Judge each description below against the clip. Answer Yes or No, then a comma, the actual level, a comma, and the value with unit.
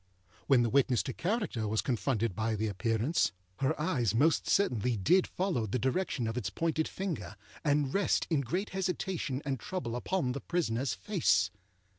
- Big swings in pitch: Yes, wide, 6.8 semitones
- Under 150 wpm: No, average, 165 wpm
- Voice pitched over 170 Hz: No, low, 135 Hz